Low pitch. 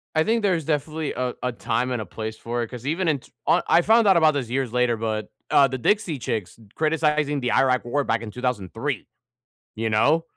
Yes: low, 130 Hz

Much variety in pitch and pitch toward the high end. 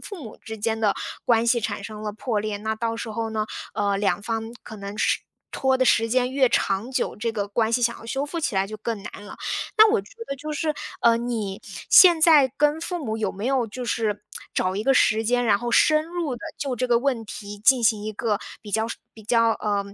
No: average, 3.5 semitones; high, 230 Hz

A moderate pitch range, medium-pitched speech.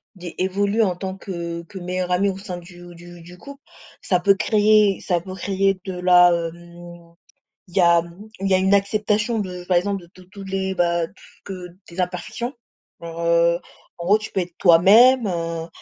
No: narrow, 2.3 semitones; medium, 180 Hz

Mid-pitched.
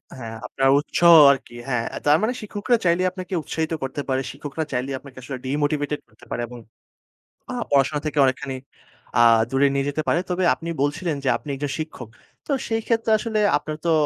Yes: medium, 145 Hz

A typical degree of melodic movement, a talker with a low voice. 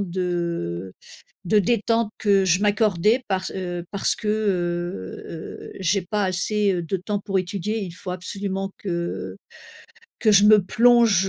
No: average, 3.0 semitones; high, 195 Hz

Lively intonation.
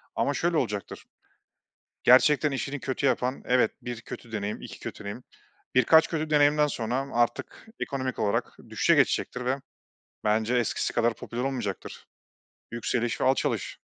No: average, 2.9 semitones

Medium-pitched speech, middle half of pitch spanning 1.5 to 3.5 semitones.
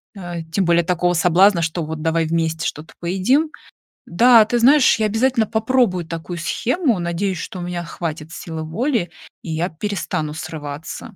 No: medium, 175 Hz; average, 4.8 semitones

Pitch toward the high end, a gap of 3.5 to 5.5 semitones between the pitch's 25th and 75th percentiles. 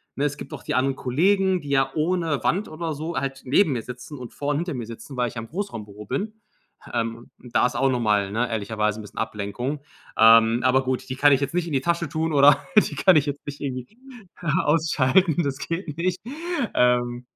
No: low, 135 Hz; average, 4.8 semitones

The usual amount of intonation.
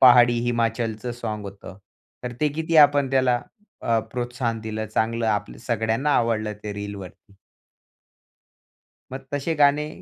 Yes: average, 3.2 semitones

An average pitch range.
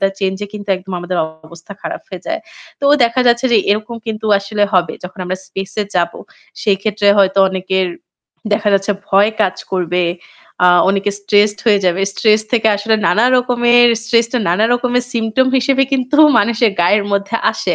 Yes: average, 3.5 semitones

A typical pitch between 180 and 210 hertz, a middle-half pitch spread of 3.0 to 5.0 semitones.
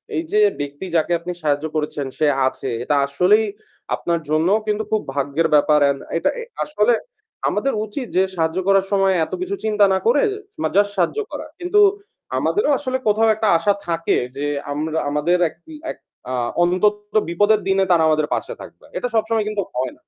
No: high, 190 Hz; wide, 5.6 semitones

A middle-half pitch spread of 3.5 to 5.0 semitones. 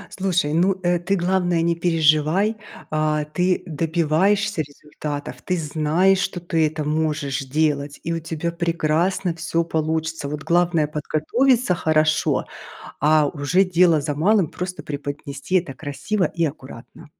No: average, 2.8 semitones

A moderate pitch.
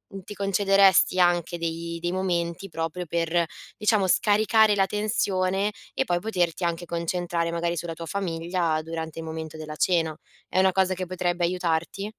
Yes: medium, 175 Hz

